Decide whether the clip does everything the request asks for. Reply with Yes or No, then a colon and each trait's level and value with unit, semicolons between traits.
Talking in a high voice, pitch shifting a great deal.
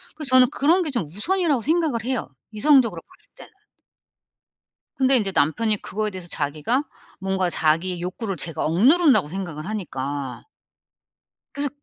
Yes: high, 215 Hz; wide, 7.7 semitones